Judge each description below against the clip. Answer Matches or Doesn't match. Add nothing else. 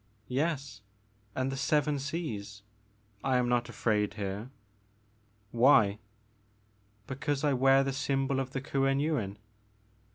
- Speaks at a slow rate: Matches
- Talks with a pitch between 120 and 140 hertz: Matches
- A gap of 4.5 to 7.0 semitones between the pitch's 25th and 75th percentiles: Doesn't match